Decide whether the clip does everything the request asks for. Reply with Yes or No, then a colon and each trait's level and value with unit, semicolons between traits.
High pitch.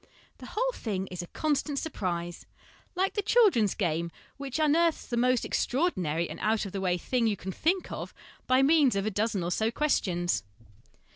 Yes: high, 225 Hz